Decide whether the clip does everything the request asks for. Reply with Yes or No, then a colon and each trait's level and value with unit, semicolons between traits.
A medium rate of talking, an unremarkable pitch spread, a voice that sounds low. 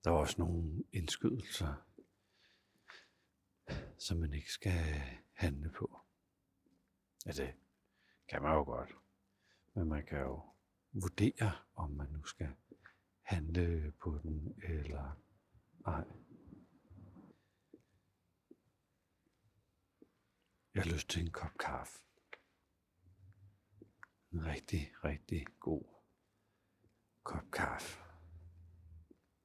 No: slow, 90 wpm; average, 3.4 semitones; very low, 85 Hz